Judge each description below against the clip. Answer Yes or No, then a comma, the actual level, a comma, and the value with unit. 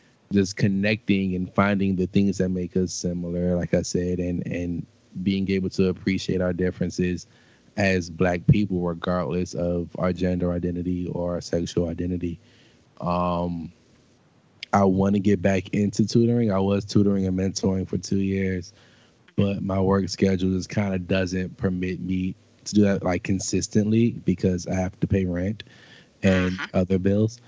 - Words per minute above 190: No, average, 160 wpm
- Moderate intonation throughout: No, narrow, 1.8 semitones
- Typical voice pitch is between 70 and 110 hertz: Yes, very low, 95 Hz